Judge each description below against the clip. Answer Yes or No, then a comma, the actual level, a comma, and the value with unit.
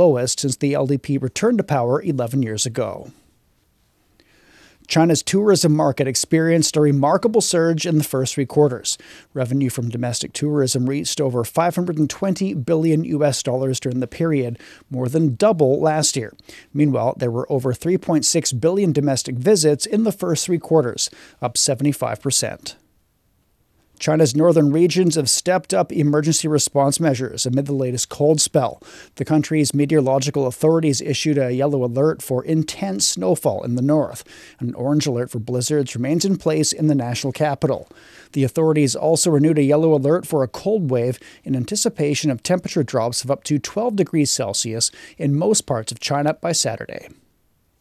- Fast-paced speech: No, average, 155 wpm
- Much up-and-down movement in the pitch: No, average, 3.6 semitones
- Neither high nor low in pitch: Yes, medium, 145 Hz